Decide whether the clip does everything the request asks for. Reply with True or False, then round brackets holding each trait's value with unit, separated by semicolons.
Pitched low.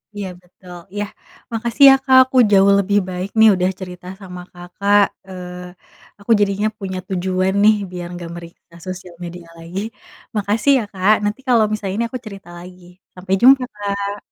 False (195 Hz)